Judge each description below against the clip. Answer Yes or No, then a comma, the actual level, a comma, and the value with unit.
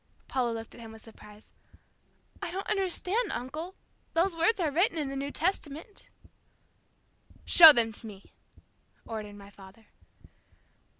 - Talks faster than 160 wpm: No, slow, 135 wpm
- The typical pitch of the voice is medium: No, very high, 280 Hz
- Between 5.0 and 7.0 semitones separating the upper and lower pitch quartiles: No, wide, 7.8 semitones